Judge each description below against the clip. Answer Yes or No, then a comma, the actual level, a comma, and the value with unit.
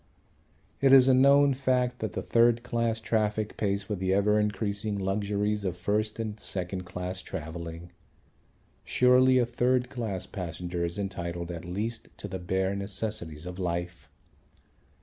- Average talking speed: Yes, average, 150 wpm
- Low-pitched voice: Yes, low, 100 Hz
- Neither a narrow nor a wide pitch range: Yes, average, 4.3 semitones